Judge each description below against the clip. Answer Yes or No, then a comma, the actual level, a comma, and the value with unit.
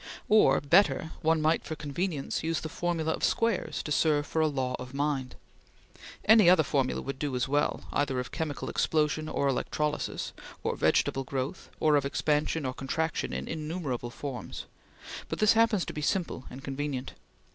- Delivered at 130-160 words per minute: No, average, 170 wpm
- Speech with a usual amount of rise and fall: Yes, average, 3.0 semitones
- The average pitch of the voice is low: No, medium, 150 Hz